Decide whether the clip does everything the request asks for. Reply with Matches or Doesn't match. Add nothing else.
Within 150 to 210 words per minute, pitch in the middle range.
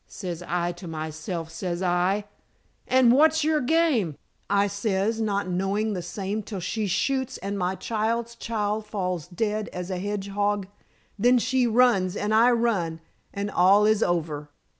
Doesn't match